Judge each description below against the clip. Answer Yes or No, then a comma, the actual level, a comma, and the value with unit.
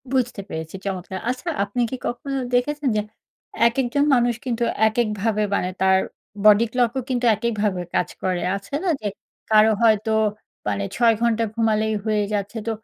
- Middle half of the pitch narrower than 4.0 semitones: Yes, average, 3.1 semitones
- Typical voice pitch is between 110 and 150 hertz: No, high, 220 Hz